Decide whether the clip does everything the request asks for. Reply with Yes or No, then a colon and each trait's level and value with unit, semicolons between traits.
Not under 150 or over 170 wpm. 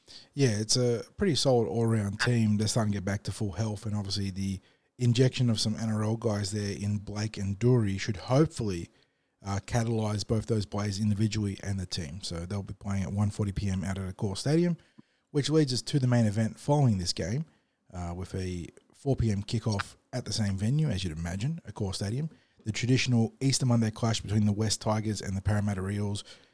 No: average, 200 wpm